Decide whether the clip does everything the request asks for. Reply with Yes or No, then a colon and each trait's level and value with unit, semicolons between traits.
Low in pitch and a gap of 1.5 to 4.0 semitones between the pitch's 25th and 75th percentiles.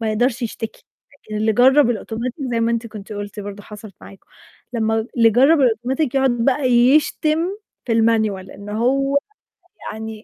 No: high, 230 Hz; average, 3.0 semitones